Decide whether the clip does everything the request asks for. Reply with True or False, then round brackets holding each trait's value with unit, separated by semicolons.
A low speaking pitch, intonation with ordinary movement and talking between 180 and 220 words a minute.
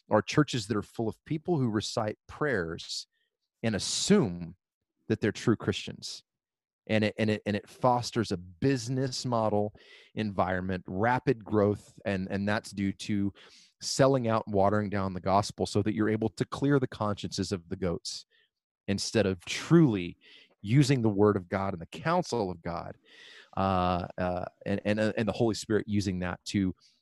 False (105 Hz; 3.7 semitones; 170 wpm)